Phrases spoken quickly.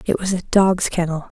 Yes: fast, 215 wpm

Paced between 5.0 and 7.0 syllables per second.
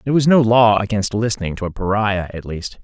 Yes: 5.9 syllables/s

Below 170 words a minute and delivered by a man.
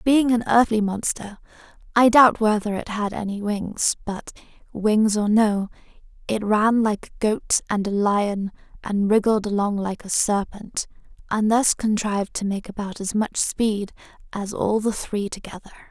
No: average, 160 wpm; female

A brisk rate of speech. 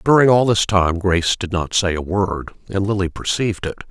Yes: fast, 230 wpm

